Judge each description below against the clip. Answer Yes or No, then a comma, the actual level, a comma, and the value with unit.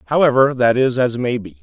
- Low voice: Yes, low, 125 Hz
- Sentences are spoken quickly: Yes, fast, 220 wpm